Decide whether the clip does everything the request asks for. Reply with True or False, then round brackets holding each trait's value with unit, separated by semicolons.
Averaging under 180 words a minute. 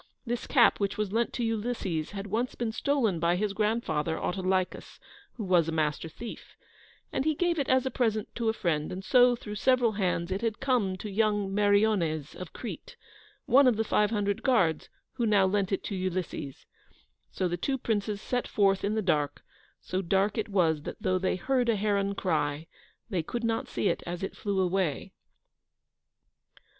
False (190 wpm)